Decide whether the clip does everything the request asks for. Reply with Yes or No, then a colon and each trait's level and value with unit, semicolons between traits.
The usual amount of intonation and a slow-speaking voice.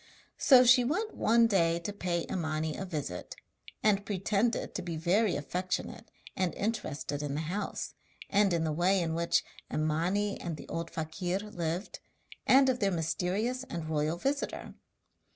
No: average, 4.4 semitones; average, 155 wpm